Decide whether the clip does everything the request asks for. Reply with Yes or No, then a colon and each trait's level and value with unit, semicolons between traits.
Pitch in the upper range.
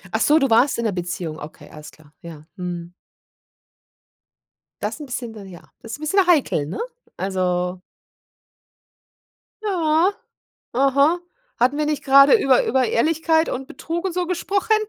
Yes: very high, 265 Hz